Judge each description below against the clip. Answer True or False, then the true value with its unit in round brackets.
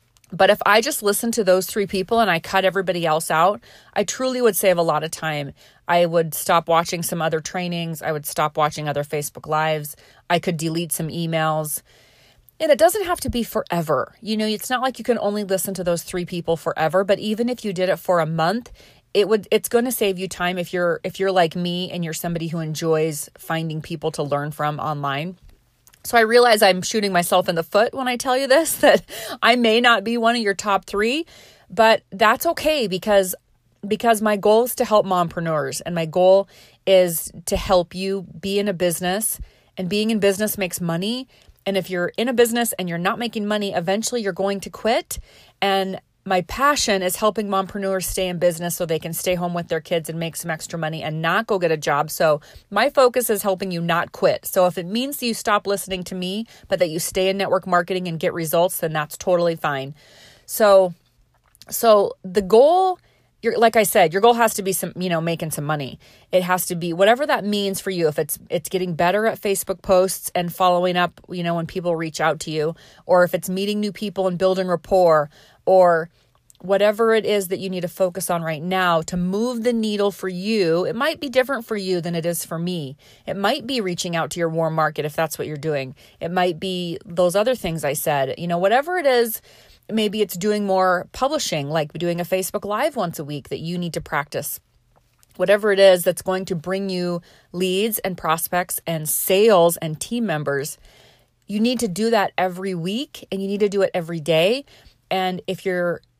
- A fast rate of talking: True (220 wpm)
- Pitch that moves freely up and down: False (3.9 semitones)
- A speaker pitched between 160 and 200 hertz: True (185 Hz)